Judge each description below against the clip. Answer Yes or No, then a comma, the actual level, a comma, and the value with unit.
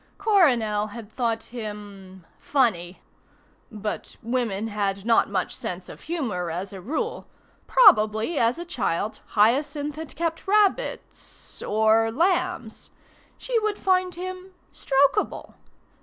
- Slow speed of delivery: Yes, slow, 115 wpm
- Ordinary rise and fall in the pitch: No, wide, 8.6 semitones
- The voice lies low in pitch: No, high, 235 Hz